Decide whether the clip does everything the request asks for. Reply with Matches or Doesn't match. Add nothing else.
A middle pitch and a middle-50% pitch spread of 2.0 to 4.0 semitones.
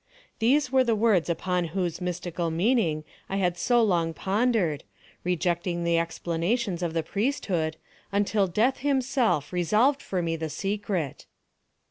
Doesn't match